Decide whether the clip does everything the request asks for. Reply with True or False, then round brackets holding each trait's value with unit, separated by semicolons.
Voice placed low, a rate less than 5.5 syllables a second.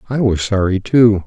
True (105 Hz; 4.7 syllables/s)